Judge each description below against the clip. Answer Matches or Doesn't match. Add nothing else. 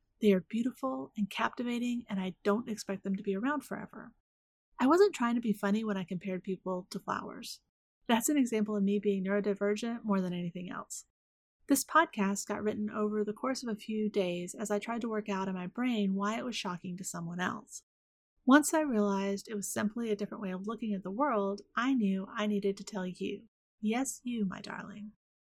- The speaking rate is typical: Doesn't match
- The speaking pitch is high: Matches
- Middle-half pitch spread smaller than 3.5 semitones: Matches